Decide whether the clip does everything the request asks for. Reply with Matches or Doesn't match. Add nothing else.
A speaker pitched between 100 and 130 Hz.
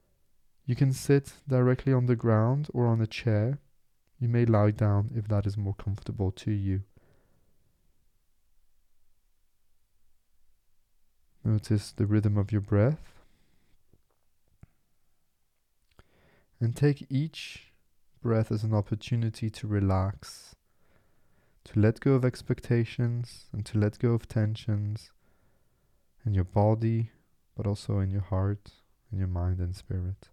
Matches